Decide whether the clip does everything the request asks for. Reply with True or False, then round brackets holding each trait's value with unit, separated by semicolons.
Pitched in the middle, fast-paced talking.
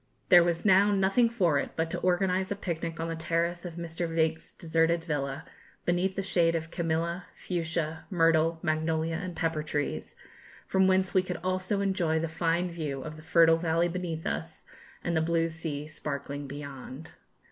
False (165 Hz; 175 wpm)